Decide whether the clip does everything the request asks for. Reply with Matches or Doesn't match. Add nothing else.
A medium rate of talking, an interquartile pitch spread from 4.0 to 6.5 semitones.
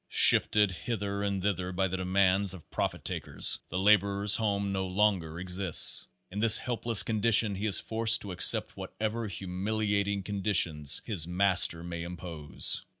Doesn't match